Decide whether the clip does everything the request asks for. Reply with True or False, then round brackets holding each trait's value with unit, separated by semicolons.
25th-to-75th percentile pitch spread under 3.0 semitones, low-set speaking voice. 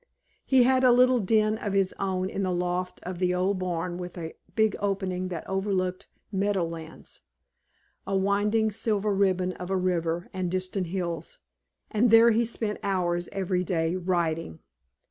False (2.4 semitones; 185 Hz)